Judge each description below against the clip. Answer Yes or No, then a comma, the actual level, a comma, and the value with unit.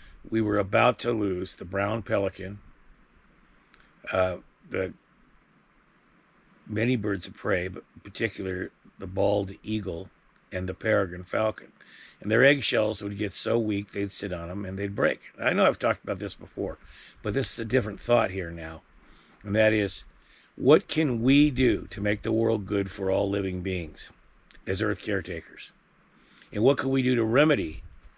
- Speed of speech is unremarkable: Yes, average, 170 wpm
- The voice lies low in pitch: Yes, low, 100 Hz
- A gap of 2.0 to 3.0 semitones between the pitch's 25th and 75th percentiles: Yes, average, 2.7 semitones